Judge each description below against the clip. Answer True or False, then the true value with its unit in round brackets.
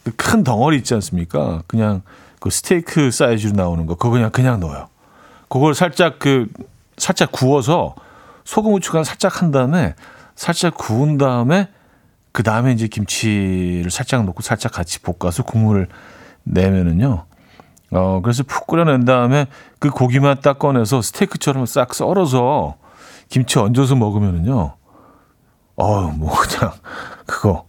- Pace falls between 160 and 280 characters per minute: False (295 characters per minute)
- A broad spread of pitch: True (6.6 semitones)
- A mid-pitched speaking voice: False (125 Hz)